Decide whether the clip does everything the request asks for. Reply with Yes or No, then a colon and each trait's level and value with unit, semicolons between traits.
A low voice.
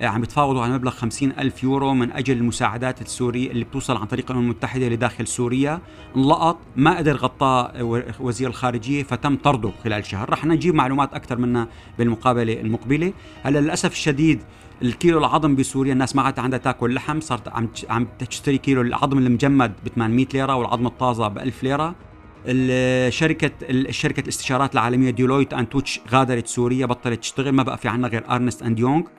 Yes: low, 130 Hz